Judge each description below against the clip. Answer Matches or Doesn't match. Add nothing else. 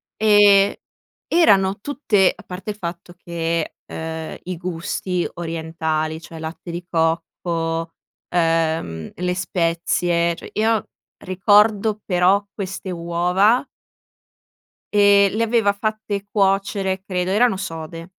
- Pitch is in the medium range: Matches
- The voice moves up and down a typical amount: Matches